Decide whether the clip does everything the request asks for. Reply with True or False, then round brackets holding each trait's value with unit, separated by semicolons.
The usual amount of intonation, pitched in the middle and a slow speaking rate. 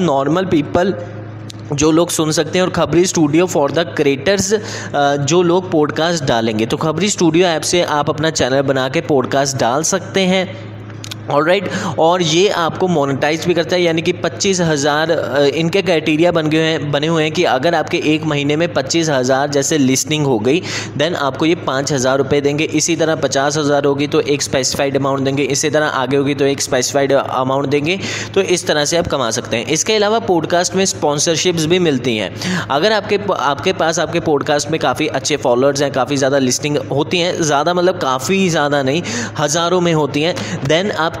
False (3.7 semitones; 155 Hz; 190 wpm)